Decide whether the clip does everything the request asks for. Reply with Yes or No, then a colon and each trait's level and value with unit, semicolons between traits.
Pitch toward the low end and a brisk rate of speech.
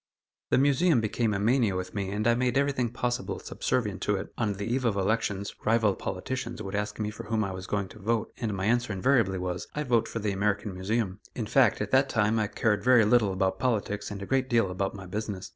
Yes: low, 105 Hz; fast, 235 wpm